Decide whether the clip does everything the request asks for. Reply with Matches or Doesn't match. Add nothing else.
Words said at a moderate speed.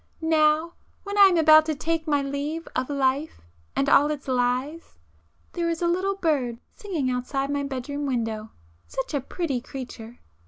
Matches